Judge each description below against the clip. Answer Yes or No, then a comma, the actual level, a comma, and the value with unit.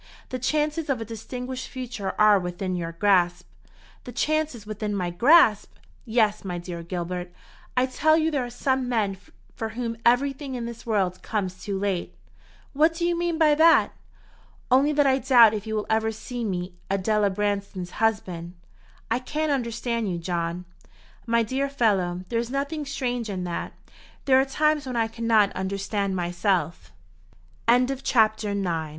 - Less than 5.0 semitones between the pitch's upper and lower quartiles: No, average, 5.3 semitones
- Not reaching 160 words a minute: No, average, 165 wpm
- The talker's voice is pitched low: No, high, 225 Hz